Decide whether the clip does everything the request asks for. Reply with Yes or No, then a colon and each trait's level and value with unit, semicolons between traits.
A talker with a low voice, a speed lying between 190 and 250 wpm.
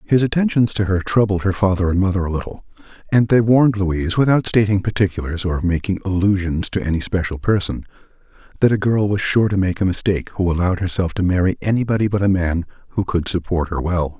Yes: very low, 95 Hz; fast, 205 wpm